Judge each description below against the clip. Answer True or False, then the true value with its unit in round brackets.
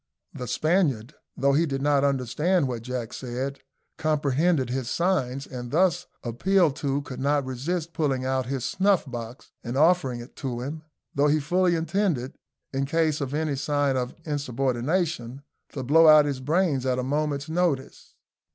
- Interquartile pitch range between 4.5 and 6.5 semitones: False (3.7 semitones)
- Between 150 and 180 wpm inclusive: True (160 wpm)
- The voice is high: False (140 Hz)